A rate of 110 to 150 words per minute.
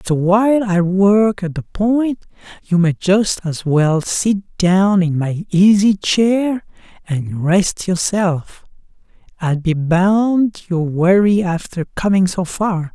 Yes: average, 140 wpm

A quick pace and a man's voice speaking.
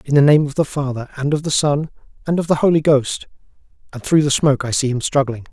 Yes: fast, 250 wpm; male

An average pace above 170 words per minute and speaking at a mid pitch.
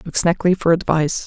No: average, 145 wpm; medium, 170 Hz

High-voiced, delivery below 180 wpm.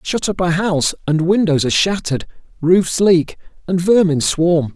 No: medium, 170 Hz; average, 165 wpm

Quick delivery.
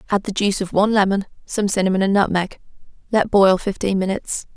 No: average, 185 wpm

